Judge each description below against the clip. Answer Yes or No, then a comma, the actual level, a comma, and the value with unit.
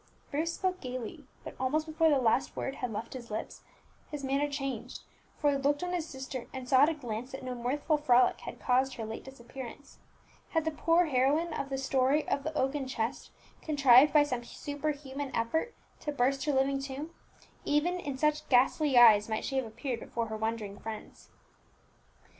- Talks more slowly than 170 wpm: No, average, 190 wpm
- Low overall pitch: No, very high, 270 Hz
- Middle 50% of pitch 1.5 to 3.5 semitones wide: Yes, average, 3.0 semitones